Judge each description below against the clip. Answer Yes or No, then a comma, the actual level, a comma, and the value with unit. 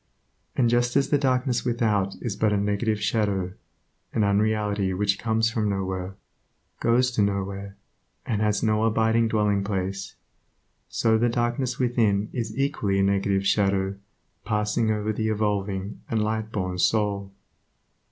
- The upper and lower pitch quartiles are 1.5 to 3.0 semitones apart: Yes, narrow, 2.4 semitones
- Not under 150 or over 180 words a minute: No, average, 140 wpm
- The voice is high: No, low, 105 Hz